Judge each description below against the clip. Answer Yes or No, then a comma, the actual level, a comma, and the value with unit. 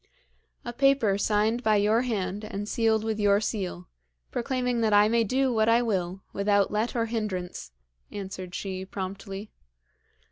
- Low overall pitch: No, high, 210 Hz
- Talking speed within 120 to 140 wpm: No, average, 150 wpm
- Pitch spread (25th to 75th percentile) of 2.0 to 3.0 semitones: Yes, average, 2.7 semitones